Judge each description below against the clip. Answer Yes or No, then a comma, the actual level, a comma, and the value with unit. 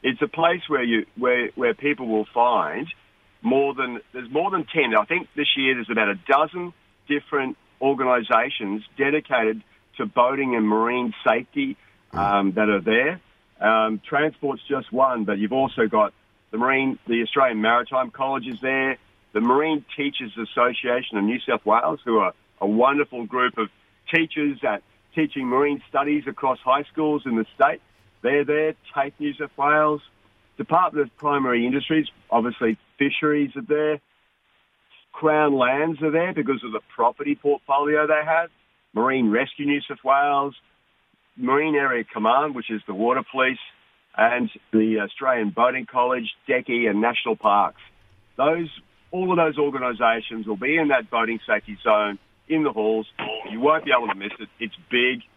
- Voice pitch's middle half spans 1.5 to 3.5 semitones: No, average, 4.5 semitones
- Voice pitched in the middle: No, low, 130 Hz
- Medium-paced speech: Yes, average, 160 wpm